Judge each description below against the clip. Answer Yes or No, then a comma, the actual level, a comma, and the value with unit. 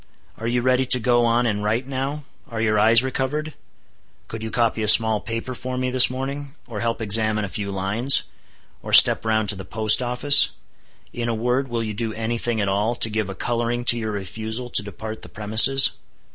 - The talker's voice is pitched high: No, low, 115 Hz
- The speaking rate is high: Yes, fast, 210 wpm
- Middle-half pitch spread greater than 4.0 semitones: No, narrow, 2.6 semitones